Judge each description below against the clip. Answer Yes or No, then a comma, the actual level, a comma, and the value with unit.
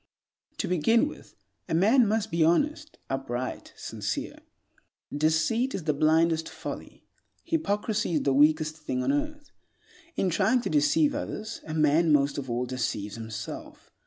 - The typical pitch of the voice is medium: Yes, medium, 160 Hz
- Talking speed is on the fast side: No, average, 145 wpm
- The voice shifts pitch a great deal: Yes, wide, 7.9 semitones